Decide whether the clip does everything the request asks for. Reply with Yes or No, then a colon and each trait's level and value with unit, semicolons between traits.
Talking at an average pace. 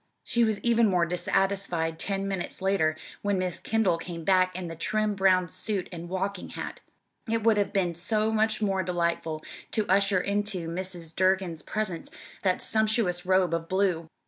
Yes: average, 170 wpm